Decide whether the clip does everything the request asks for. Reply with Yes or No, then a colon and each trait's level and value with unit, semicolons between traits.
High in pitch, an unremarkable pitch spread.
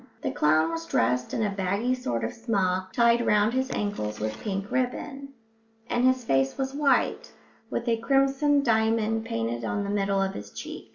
No: high, 210 Hz; wide, 6.2 semitones